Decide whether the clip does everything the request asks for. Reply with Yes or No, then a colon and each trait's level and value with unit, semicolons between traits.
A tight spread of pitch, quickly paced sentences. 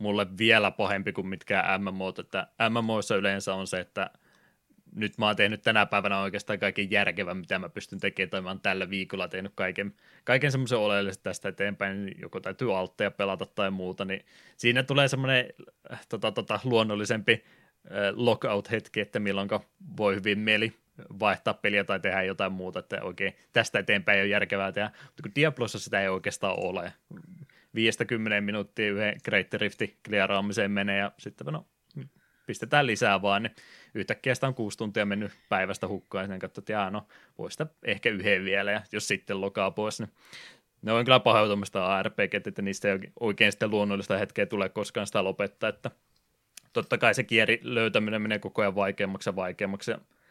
Yes: narrow, 2.1 semitones; fast, 165 wpm